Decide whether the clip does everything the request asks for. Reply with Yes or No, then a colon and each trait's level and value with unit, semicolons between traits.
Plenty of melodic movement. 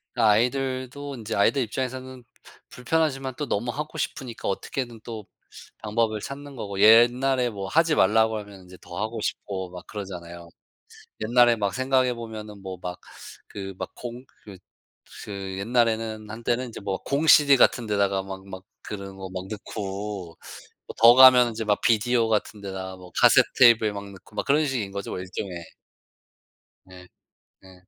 No: average, 4.2 semitones